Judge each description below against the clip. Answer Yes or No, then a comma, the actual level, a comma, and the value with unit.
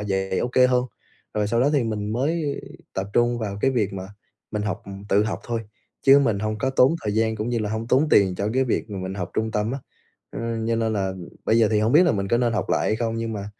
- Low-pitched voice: Yes, low, 110 Hz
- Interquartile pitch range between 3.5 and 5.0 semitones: No, average, 2.7 semitones